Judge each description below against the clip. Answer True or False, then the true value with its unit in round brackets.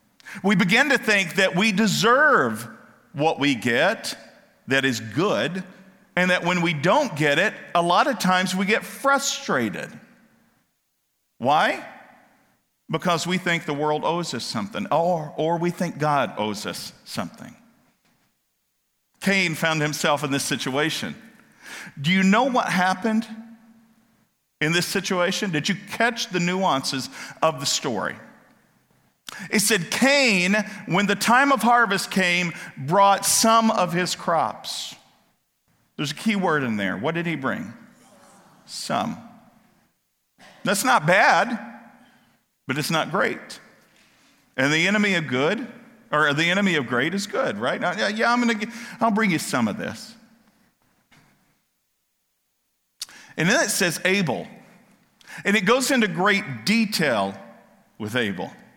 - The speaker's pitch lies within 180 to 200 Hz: True (190 Hz)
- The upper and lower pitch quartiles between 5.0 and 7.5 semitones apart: True (5.5 semitones)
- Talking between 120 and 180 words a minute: True (135 wpm)